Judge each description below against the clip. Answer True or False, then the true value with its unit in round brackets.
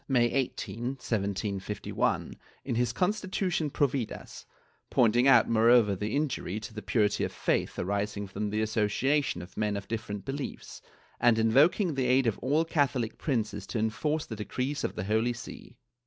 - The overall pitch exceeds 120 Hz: False (115 Hz)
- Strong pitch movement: False (4.3 semitones)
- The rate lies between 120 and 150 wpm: False (160 wpm)